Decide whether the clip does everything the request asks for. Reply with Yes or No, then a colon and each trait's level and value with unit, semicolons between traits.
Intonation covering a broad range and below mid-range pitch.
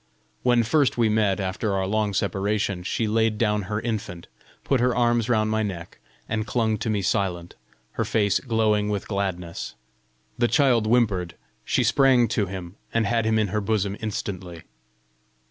No: average, 2.7 semitones; low, 105 Hz